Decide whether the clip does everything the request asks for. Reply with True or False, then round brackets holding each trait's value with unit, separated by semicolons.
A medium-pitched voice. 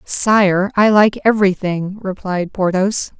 False (195 Hz)